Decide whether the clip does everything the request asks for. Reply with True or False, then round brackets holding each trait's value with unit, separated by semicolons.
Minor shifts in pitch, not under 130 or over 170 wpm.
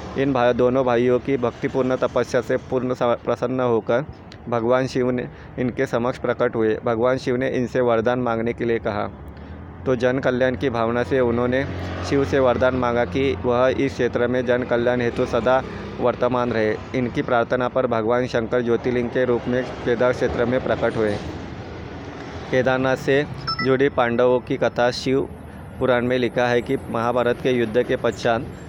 True (1.6 semitones; 165 wpm)